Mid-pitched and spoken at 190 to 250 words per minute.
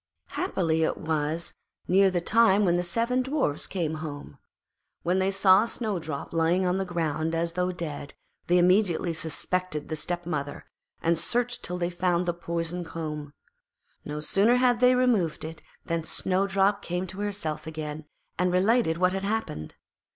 No: medium, 175 Hz; average, 160 wpm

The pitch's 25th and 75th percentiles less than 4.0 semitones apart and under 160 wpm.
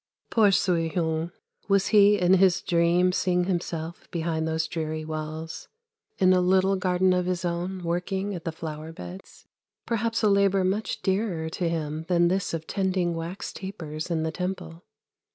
No: average, 2.8 semitones; average, 165 wpm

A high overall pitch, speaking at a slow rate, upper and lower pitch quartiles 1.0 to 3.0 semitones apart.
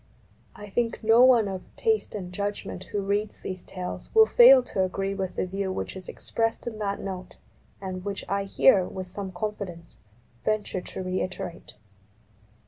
No: high, 195 Hz; average, 165 wpm; narrow, 2.4 semitones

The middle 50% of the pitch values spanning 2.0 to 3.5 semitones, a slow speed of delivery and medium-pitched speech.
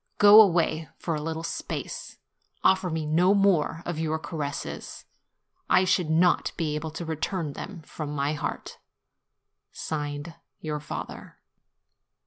Yes: average, 2.8 semitones; slow, 125 wpm; medium, 160 Hz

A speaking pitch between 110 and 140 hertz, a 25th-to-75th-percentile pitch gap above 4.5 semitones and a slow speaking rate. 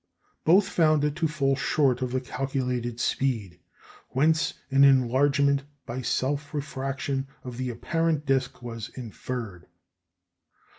No: low, 135 Hz; average, 2.7 semitones; slow, 120 wpm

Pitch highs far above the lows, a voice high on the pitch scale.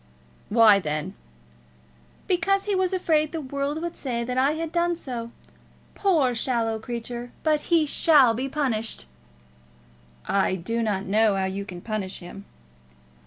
Yes: wide, 6.4 semitones; high, 245 Hz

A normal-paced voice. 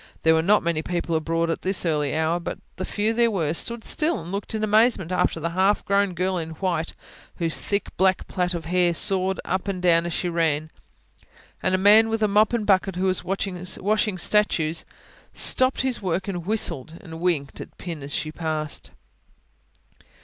Yes: average, 190 wpm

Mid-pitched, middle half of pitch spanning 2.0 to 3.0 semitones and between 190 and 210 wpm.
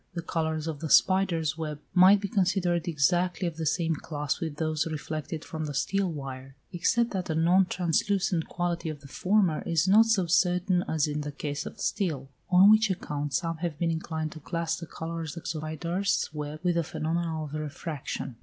Yes: medium, 165 Hz; average, 2.7 semitones; average, 195 wpm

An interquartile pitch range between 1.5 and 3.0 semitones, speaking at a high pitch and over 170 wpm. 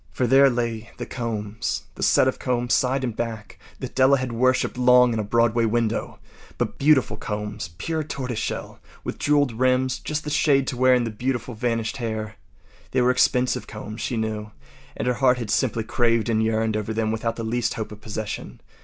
No: narrow, 2.5 semitones; low, 120 Hz; average, 190 wpm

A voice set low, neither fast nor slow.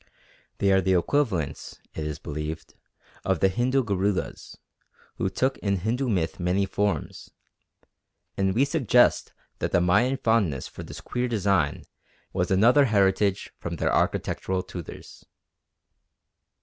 No: very low, 95 Hz; slow, 130 wpm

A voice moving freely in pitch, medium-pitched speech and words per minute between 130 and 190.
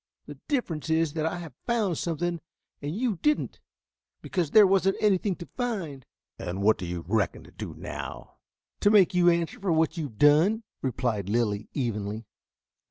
Yes: wide, 8.3 semitones; medium, 160 Hz; average, 170 wpm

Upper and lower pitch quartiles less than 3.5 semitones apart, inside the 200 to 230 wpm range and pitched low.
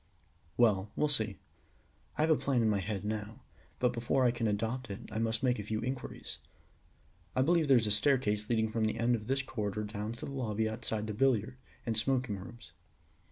Yes: average, 3.1 semitones; fast, 205 wpm; low, 115 Hz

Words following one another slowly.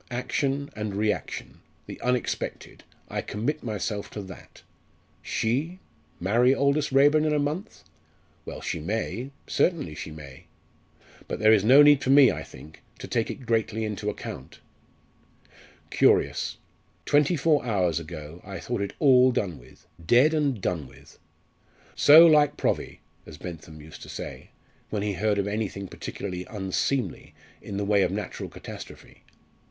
No: average, 150 wpm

